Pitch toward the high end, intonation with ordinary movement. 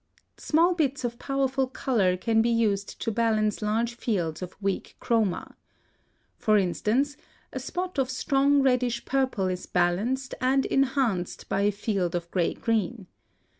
Yes: high, 230 Hz; average, 5.0 semitones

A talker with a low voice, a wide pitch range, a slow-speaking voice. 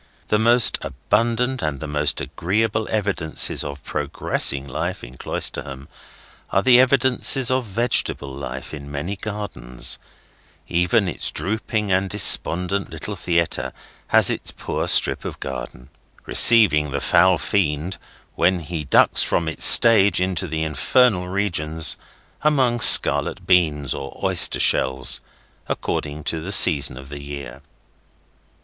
Yes: very low, 85 Hz; wide, 6.6 semitones; slow, 130 wpm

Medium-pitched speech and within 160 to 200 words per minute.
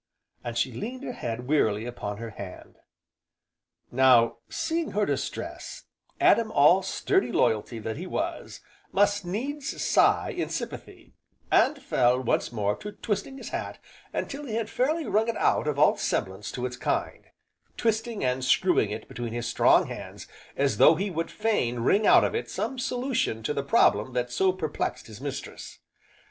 Yes: medium, 150 Hz; average, 165 wpm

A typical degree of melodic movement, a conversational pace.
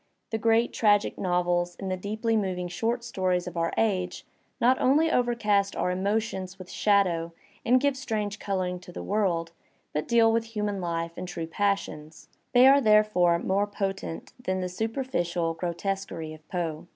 Yes: average, 3.9 semitones; average, 165 wpm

